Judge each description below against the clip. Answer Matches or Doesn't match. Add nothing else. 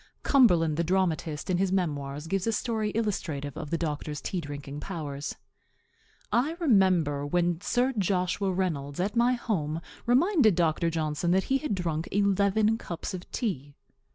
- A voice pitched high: Doesn't match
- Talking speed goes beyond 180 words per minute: Doesn't match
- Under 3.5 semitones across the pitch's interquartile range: Doesn't match